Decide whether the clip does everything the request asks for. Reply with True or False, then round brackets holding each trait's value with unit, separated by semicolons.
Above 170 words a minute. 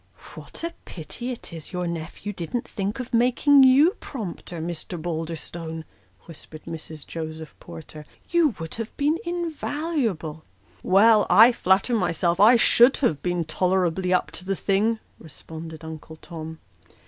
False (150 wpm)